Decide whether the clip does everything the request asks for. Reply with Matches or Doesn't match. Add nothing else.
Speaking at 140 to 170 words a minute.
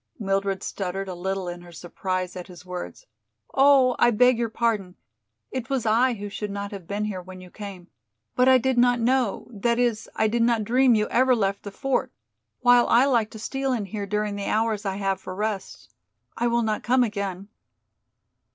Doesn't match